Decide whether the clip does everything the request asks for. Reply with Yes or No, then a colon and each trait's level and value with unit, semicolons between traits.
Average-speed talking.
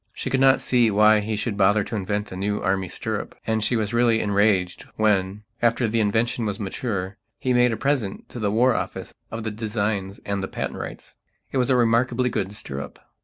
No: fast, 210 wpm